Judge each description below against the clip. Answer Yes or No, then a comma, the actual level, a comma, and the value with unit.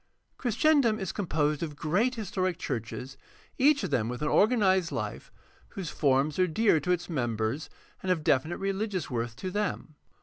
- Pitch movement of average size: No, wide, 6.1 semitones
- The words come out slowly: No, average, 170 wpm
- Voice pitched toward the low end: No, medium, 175 Hz